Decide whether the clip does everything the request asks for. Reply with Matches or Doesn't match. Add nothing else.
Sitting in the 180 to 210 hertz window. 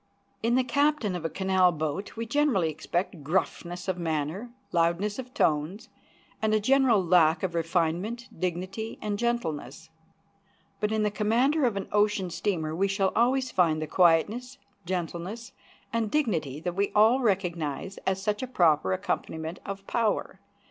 Matches